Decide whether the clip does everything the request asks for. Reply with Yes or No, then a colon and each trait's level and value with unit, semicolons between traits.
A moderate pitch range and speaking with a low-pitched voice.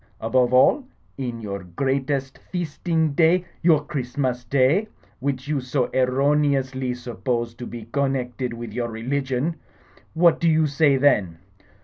Yes: average, 3.0 semitones; low, 130 Hz